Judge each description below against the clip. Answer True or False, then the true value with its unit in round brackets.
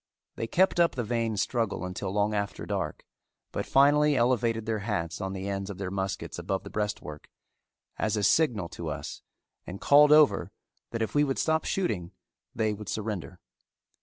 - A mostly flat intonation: False (4.2 semitones)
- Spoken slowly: False (175 wpm)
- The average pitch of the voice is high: False (105 Hz)